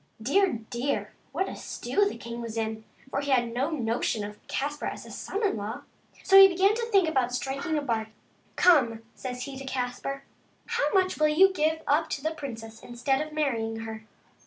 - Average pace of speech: No, fast, 210 wpm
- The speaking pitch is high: Yes, very high, 270 Hz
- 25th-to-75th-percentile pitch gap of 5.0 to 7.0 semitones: Yes, average, 5.3 semitones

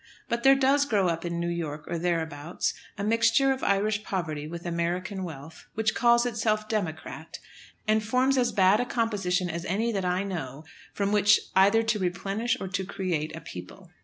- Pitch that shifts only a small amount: No, average, 4.5 semitones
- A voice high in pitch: Yes, high, 195 Hz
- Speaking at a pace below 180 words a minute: No, average, 185 wpm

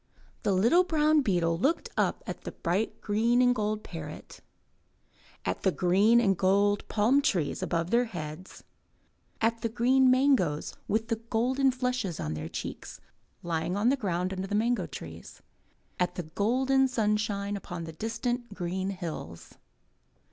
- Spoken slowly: No, average, 150 wpm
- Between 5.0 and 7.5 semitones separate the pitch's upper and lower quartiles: Yes, wide, 5.6 semitones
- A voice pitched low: No, high, 205 Hz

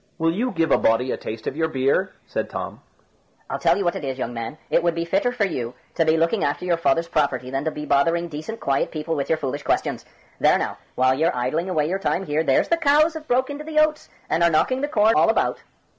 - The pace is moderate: No, fast, 255 wpm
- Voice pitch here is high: No, medium, 165 Hz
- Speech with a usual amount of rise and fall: No, wide, 6.3 semitones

